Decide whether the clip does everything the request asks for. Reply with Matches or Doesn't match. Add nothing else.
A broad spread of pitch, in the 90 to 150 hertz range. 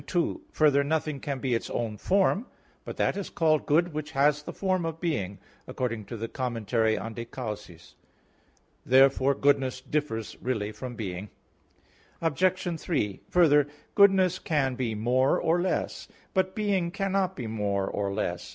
Matches